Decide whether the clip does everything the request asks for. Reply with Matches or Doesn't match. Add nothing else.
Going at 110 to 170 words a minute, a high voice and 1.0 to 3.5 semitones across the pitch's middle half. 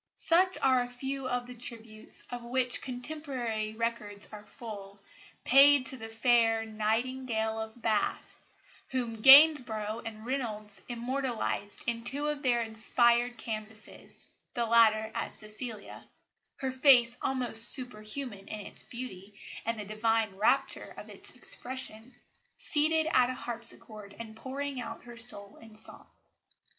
Matches